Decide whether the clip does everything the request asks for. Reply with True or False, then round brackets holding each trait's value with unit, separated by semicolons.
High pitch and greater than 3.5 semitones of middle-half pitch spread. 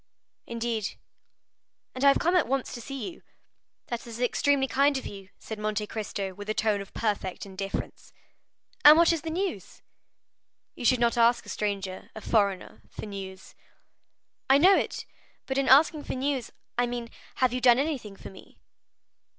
True (235 Hz; 4.8 semitones)